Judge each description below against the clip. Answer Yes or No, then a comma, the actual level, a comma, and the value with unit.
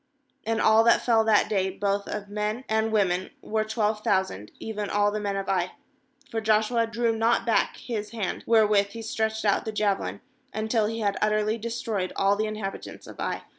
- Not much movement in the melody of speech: Yes, narrow, 1.7 semitones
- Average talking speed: Yes, average, 195 wpm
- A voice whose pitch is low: No, high, 215 Hz